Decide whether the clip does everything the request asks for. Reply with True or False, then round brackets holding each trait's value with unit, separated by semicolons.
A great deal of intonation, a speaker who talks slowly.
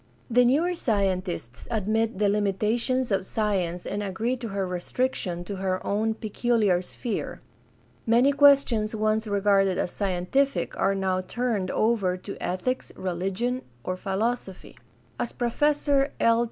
False (4.2 semitones; 130 wpm)